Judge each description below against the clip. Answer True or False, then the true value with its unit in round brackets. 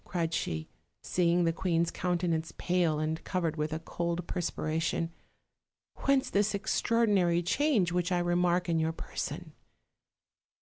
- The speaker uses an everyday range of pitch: False (1.8 semitones)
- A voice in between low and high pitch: True (175 Hz)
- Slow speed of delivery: True (130 wpm)